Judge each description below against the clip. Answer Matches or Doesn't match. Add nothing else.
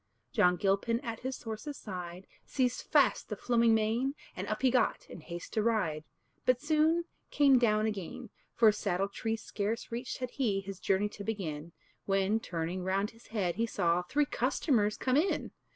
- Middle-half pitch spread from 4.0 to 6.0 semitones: Matches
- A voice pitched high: Matches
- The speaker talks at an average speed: Matches